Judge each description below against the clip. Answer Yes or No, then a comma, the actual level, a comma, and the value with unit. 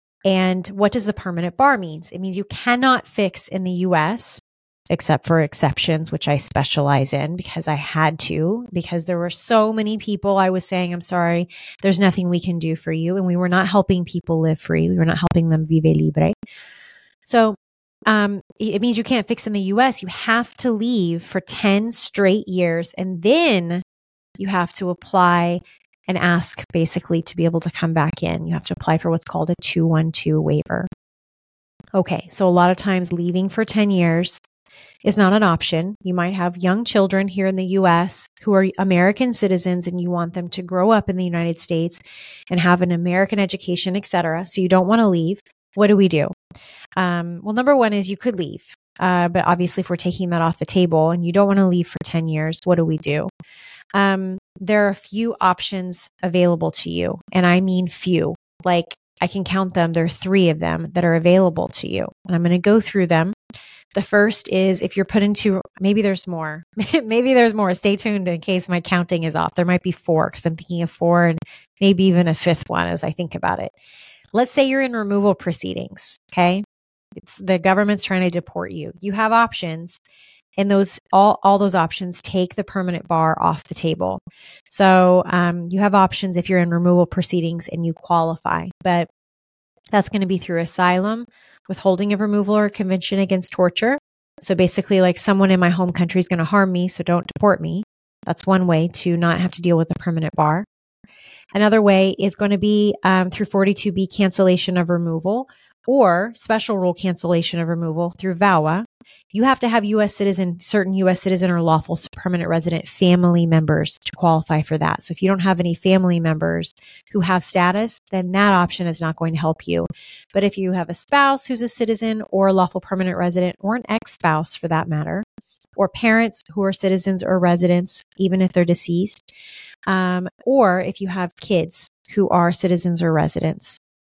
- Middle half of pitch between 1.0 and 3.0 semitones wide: Yes, average, 2.7 semitones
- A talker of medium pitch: Yes, medium, 180 Hz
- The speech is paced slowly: No, average, 200 wpm